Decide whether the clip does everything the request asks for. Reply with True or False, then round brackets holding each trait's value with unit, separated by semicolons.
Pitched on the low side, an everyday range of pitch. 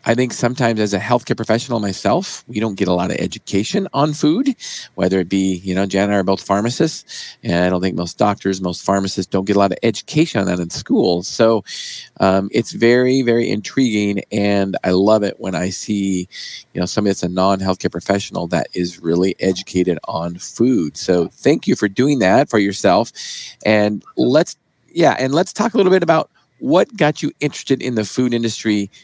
True (100 Hz; 4.1 semitones)